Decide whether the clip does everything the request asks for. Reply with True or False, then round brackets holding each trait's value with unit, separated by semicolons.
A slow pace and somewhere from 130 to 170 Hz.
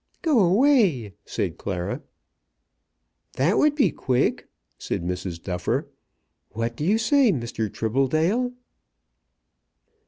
True (100 wpm; 140 Hz)